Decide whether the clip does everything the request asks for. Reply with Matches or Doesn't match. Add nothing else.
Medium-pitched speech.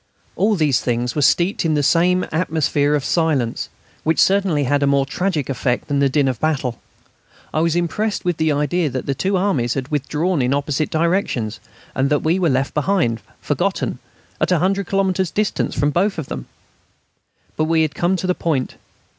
Matches